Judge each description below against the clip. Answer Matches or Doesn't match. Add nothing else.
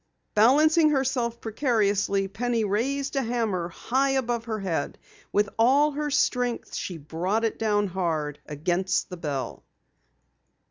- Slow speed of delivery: Matches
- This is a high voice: Matches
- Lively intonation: Matches